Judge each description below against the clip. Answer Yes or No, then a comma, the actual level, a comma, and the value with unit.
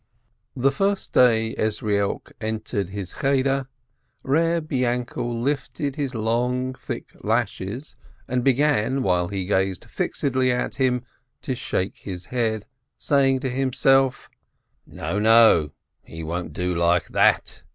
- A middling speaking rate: No, slow, 120 wpm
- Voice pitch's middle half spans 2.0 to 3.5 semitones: No, average, 4.7 semitones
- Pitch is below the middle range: Yes, low, 120 Hz